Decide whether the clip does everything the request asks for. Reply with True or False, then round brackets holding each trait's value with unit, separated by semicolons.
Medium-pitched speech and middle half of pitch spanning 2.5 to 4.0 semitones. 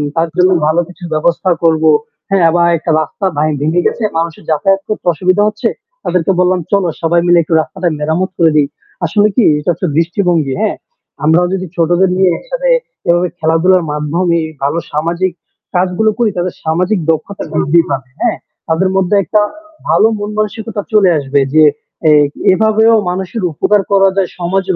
True (180 Hz; 2.9 semitones)